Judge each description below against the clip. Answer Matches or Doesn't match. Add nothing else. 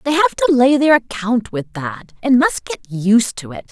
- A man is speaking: Doesn't match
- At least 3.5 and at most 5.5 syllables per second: Matches